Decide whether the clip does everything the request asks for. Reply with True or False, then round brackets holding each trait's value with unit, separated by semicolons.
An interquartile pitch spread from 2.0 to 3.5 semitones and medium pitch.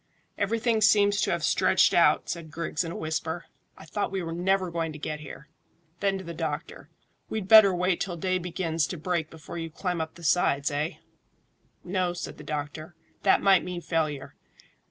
True (3.1 semitones; 170 Hz)